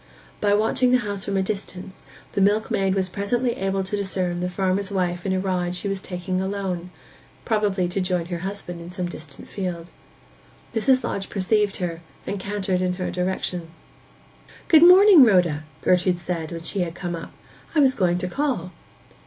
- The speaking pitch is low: No, high, 190 Hz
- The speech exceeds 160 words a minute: Yes, average, 175 wpm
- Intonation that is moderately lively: No, narrow, 2.3 semitones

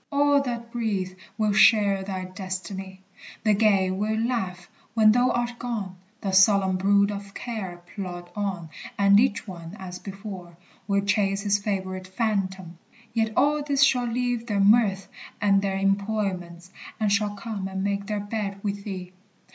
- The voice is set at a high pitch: Yes, high, 200 Hz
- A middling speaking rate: Yes, average, 155 wpm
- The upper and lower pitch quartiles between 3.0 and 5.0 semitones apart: No, narrow, 2.5 semitones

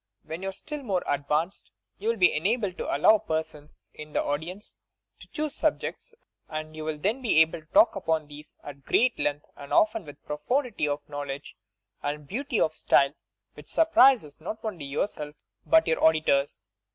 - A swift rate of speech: No, average, 185 wpm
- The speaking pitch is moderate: Yes, medium, 160 Hz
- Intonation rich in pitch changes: Yes, wide, 6.6 semitones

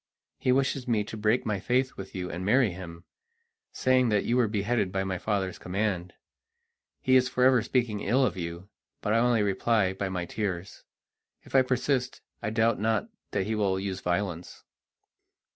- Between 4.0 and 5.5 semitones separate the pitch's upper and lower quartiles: Yes, average, 4.5 semitones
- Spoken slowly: No, average, 175 wpm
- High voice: No, low, 105 Hz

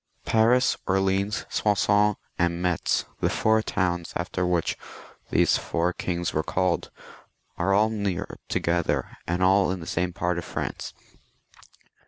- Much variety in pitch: No, average, 2.7 semitones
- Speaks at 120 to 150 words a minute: Yes, slow, 135 wpm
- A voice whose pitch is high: No, very low, 90 Hz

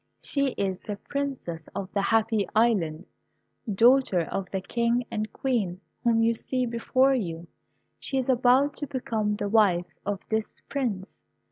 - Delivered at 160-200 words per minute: No, average, 150 wpm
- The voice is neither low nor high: No, high, 225 Hz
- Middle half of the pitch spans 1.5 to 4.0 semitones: No, average, 4.5 semitones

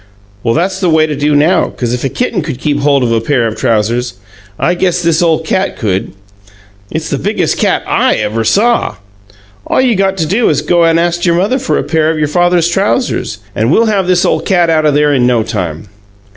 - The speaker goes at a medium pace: No, fast, 230 wpm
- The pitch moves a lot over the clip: Yes, wide, 6.3 semitones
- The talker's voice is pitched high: No, medium, 160 Hz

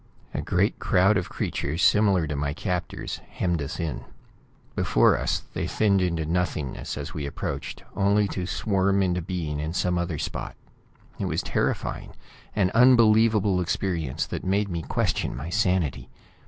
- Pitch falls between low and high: No, very low, 90 Hz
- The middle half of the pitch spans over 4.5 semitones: No, average, 3.7 semitones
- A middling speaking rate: Yes, average, 155 wpm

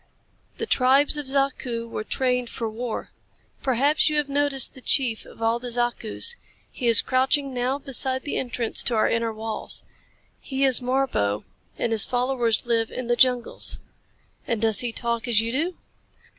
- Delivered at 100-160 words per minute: No, average, 170 wpm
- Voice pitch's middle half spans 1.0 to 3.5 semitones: Yes, average, 2.7 semitones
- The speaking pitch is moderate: No, high, 245 Hz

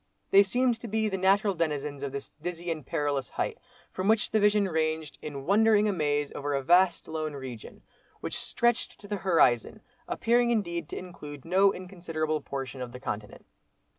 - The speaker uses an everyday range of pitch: No, wide, 5.7 semitones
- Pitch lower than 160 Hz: No, medium, 170 Hz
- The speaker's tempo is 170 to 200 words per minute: Yes, average, 175 wpm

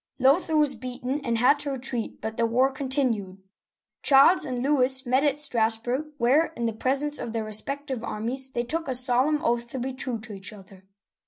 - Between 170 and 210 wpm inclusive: Yes, average, 195 wpm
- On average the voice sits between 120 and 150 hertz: No, very high, 255 Hz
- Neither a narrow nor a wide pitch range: Yes, average, 3.1 semitones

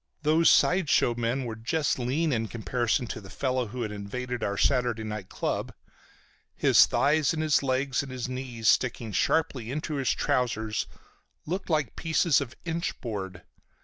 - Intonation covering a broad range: No, average, 4.3 semitones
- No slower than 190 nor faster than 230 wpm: No, average, 165 wpm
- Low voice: Yes, low, 125 Hz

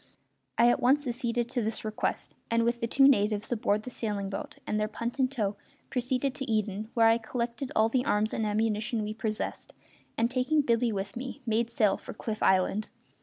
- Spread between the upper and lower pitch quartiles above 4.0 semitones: No, narrow, 2.6 semitones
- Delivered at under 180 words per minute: No, average, 200 wpm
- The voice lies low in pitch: No, high, 230 Hz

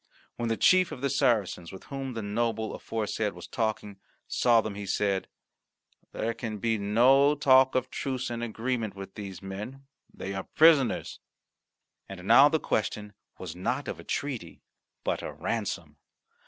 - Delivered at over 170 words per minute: No, average, 160 wpm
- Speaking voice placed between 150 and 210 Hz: No, low, 115 Hz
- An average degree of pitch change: Yes, average, 4.3 semitones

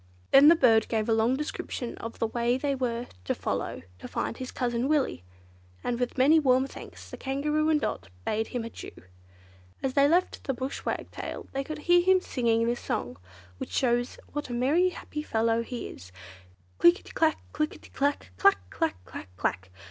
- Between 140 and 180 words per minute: No, average, 195 wpm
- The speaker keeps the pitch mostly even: No, average, 4.3 semitones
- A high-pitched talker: Yes, very high, 250 Hz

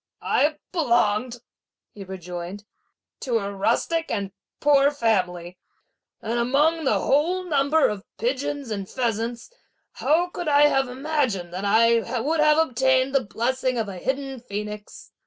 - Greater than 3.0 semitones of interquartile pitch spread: Yes, wide, 5.5 semitones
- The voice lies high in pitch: Yes, very high, 250 Hz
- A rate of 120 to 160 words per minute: Yes, average, 140 wpm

